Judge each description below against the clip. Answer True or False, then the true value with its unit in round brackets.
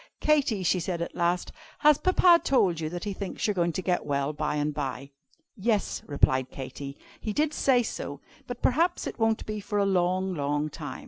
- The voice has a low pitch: False (185 Hz)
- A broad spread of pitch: True (6.9 semitones)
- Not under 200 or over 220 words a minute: True (205 wpm)